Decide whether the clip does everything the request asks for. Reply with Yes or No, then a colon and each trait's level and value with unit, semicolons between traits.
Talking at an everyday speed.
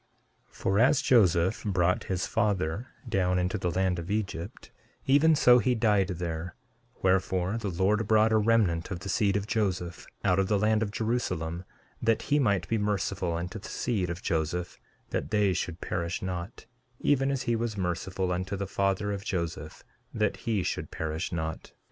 Yes: average, 180 wpm